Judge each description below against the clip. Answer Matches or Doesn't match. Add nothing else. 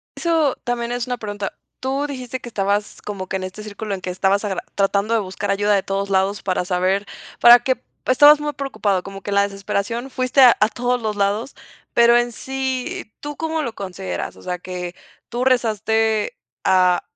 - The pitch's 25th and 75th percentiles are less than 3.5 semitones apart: Doesn't match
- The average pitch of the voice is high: Matches